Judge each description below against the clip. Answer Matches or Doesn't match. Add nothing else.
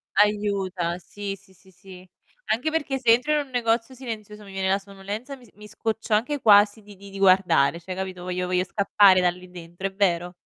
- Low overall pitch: Doesn't match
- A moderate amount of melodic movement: Matches